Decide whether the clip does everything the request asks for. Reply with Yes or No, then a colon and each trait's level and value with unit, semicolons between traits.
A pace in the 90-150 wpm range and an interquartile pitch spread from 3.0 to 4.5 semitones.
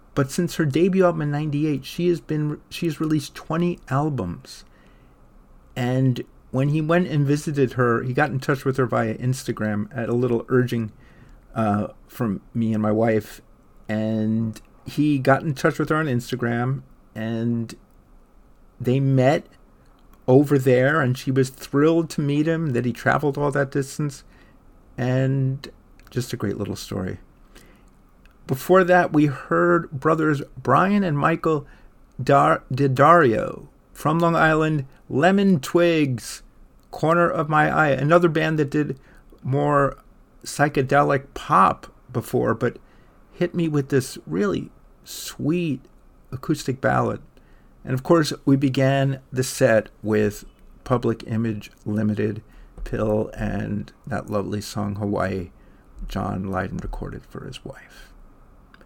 No: slow, 135 wpm; average, 5.0 semitones